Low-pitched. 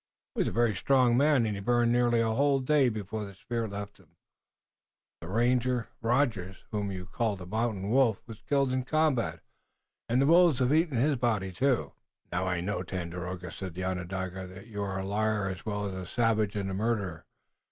Yes: low, 110 Hz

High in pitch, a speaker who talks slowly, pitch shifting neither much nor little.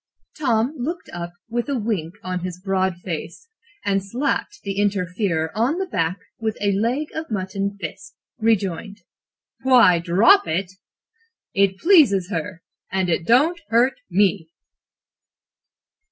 Yes: high, 200 Hz; slow, 130 wpm; average, 4.7 semitones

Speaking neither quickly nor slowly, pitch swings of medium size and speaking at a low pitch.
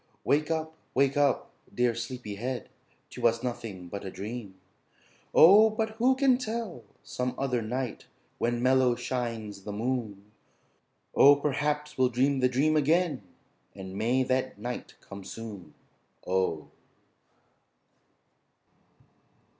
No: slow, 120 wpm; average, 4.8 semitones; low, 125 Hz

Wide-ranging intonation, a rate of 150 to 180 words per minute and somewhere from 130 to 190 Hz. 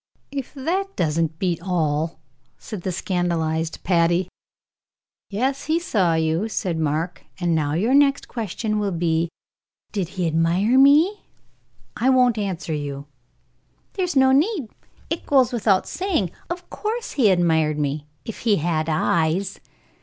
No: wide, 8.1 semitones; average, 140 wpm; medium, 185 Hz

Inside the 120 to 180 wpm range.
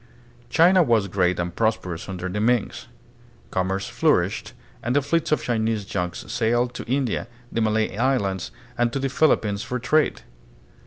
Yes: average, 160 wpm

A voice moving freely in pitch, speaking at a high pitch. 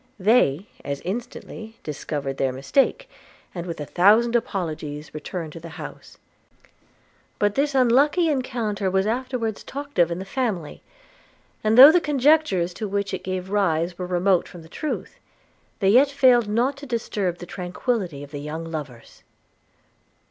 Yes: wide, 6.6 semitones; high, 195 Hz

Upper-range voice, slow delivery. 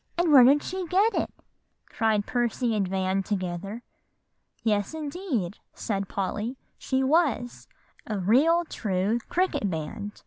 Yes: high, 225 Hz; slow, 130 wpm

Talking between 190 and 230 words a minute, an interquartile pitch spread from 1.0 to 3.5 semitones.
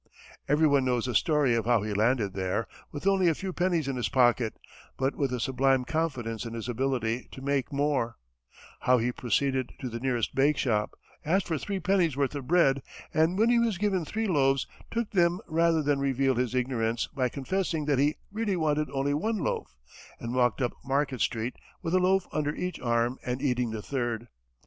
No: average, 195 wpm; average, 4.8 semitones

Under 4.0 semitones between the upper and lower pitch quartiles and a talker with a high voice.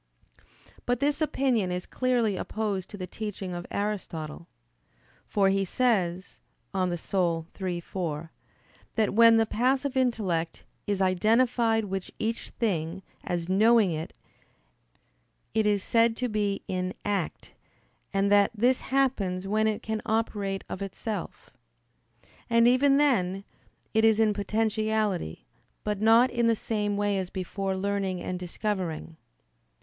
Yes: average, 3.4 semitones; high, 205 Hz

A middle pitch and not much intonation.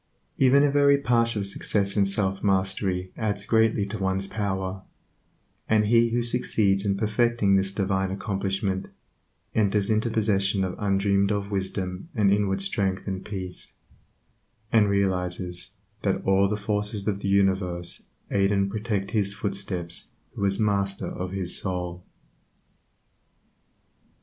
No: low, 100 Hz; narrow, 1.7 semitones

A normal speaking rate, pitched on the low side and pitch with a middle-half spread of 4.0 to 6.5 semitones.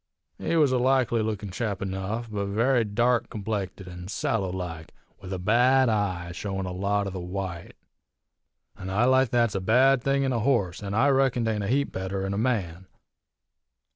Yes: average, 195 wpm; low, 105 Hz; average, 4.4 semitones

